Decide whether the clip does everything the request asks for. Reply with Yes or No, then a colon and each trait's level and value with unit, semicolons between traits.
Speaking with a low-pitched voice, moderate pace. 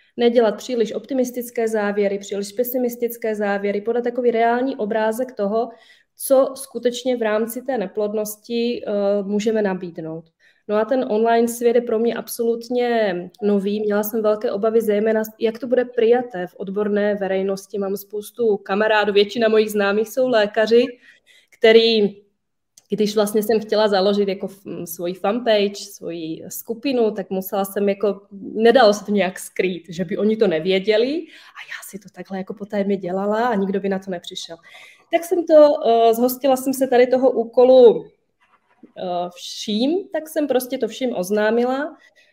No: high, 220 Hz; average, 150 wpm